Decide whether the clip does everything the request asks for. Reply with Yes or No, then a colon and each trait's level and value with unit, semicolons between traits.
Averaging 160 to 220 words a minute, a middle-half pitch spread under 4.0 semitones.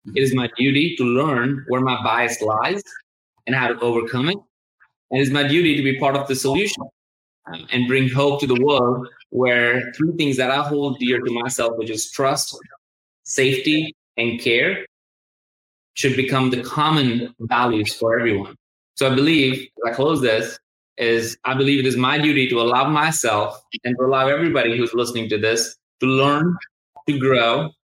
Yes: average, 175 wpm; average, 2.8 semitones